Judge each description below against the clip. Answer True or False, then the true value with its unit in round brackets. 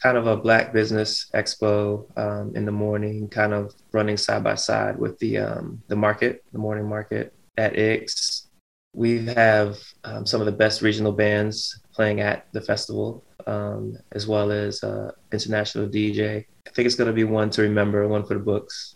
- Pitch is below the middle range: True (105 Hz)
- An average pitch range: False (0.9 semitones)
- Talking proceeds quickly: False (185 wpm)